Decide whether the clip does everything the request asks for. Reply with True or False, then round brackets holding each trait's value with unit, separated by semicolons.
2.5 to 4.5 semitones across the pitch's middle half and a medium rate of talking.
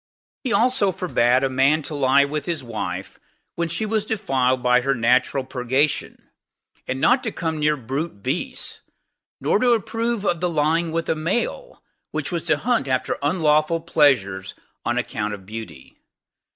False (5.2 semitones; 165 wpm)